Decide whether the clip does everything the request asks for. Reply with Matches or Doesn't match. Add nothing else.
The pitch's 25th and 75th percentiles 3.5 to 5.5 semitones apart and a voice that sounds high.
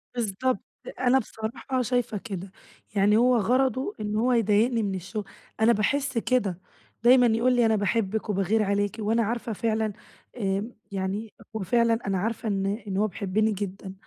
Doesn't match